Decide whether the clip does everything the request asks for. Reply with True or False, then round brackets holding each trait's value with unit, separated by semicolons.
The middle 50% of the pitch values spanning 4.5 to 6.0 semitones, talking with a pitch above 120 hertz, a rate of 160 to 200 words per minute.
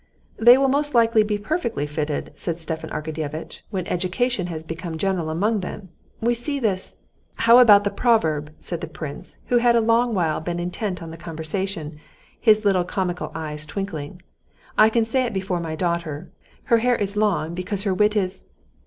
True (5.4 semitones; 185 Hz; 180 wpm)